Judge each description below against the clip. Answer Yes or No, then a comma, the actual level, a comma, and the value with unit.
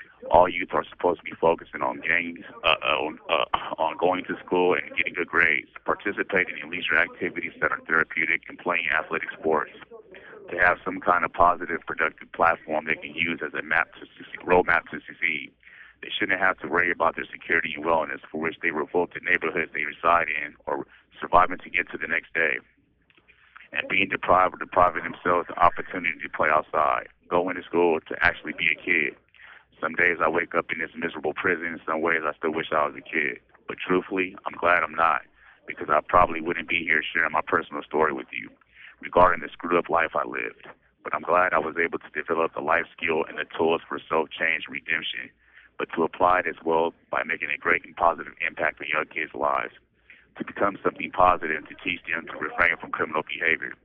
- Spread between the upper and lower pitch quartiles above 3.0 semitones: No, narrow, 2.6 semitones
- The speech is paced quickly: Yes, fast, 210 wpm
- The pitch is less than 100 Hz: Yes, very low, 85 Hz